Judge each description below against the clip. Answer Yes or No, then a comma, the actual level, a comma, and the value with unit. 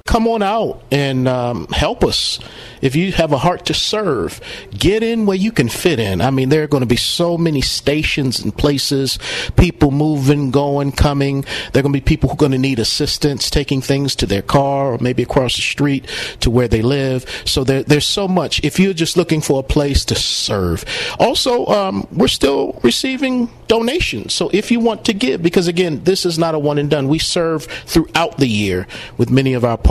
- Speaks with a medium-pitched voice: Yes, medium, 145 Hz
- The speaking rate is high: Yes, fast, 215 wpm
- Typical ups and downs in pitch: Yes, average, 4.2 semitones